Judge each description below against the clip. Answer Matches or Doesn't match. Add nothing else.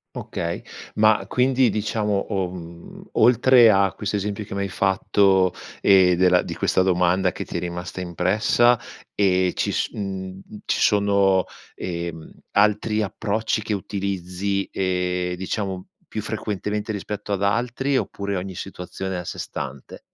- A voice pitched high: Doesn't match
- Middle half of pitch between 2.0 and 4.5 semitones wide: Matches